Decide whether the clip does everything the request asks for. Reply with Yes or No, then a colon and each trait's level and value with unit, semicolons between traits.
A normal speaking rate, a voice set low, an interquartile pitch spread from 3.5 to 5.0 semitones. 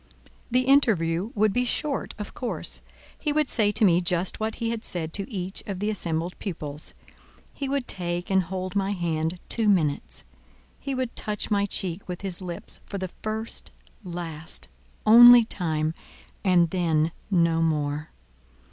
No: average, 155 wpm; high, 190 Hz; average, 4.5 semitones